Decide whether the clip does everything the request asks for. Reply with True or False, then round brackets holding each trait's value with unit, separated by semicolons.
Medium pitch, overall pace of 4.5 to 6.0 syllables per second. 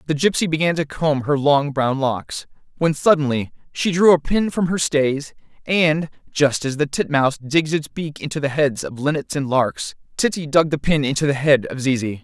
True (145 Hz; 4.9 syllables/s)